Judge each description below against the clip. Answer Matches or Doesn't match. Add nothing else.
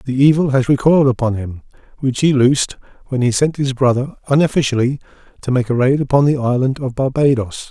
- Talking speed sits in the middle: Matches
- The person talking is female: Doesn't match